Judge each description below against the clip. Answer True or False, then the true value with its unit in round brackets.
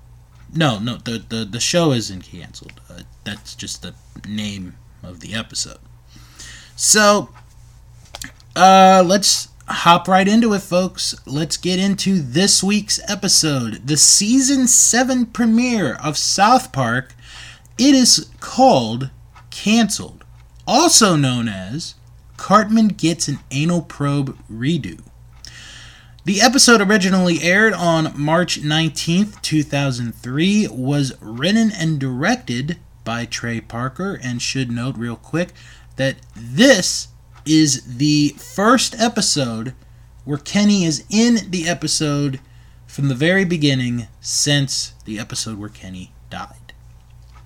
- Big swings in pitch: True (8.0 semitones)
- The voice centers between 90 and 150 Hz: True (140 Hz)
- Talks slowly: True (115 wpm)